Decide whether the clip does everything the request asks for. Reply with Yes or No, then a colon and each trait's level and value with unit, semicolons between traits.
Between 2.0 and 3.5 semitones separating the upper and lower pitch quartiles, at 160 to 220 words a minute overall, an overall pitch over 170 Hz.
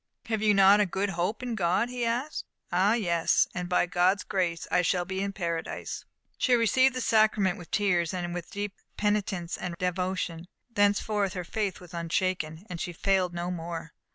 Yes: average, 2.9 semitones; average, 180 wpm; medium, 185 Hz